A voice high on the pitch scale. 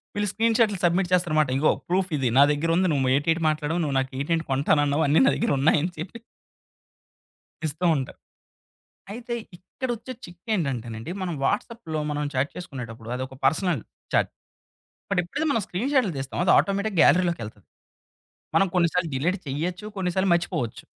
No: medium, 170 Hz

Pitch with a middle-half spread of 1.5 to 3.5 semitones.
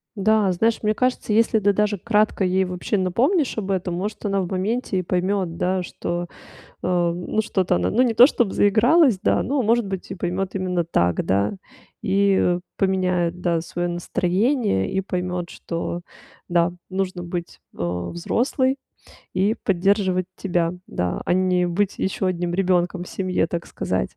Yes: average, 2.8 semitones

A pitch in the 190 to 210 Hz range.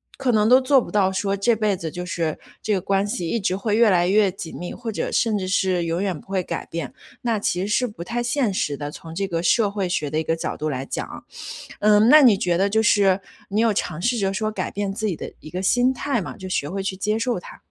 Yes: high, 195 Hz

